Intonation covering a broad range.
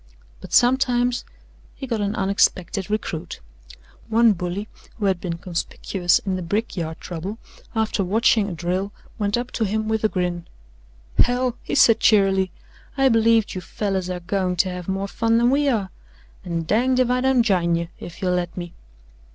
No: average, 4.1 semitones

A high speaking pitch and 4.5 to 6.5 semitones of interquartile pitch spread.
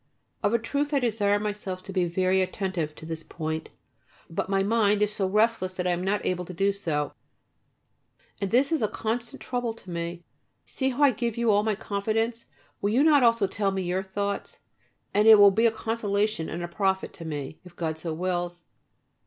No: high, 200 Hz; average, 3.8 semitones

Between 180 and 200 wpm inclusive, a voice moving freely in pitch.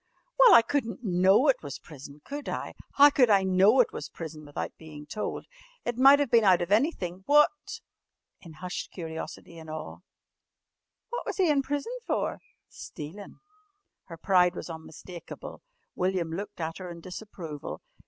No: average, 165 wpm; wide, 7.4 semitones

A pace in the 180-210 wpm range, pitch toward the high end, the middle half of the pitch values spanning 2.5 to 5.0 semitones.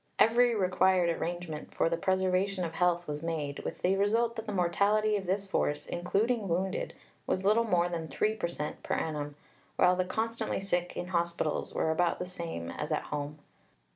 No: average, 185 wpm; medium, 180 Hz; average, 3.1 semitones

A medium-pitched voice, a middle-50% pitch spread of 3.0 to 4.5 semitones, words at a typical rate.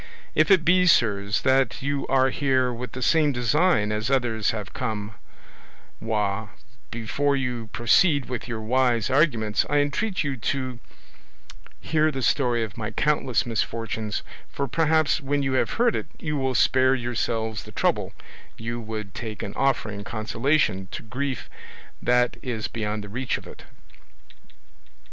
No: low, 125 Hz; average, 4.1 semitones; average, 150 wpm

